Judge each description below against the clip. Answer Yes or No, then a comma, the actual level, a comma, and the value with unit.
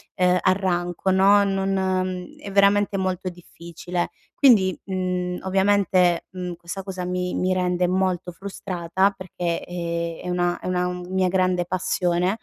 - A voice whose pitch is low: No, medium, 185 Hz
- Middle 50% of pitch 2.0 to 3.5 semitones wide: No, narrow, 1.3 semitones